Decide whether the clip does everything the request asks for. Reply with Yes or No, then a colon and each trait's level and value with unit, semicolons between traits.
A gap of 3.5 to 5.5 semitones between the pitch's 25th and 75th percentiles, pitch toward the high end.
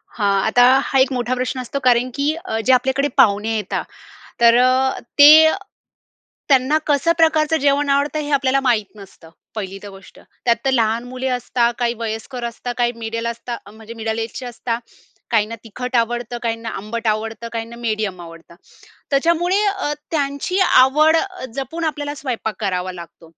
Yes: average, 3.8 semitones; high, 240 Hz